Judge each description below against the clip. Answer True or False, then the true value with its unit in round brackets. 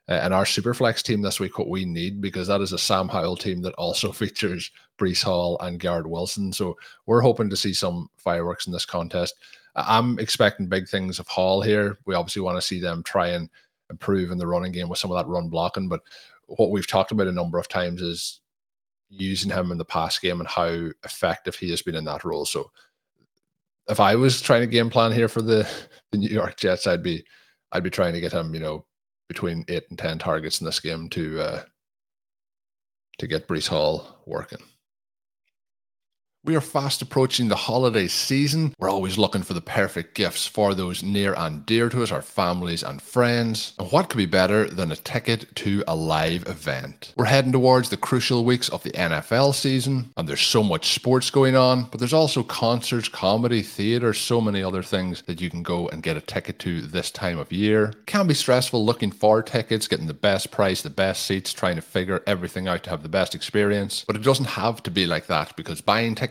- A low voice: True (100 Hz)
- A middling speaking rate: False (215 wpm)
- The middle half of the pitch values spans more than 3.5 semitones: True (5.0 semitones)